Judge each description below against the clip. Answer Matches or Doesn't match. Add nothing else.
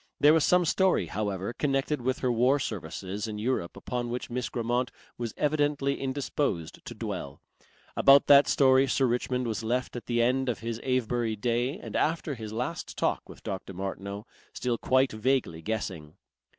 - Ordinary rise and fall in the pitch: Matches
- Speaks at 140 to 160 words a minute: Doesn't match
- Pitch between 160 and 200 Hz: Doesn't match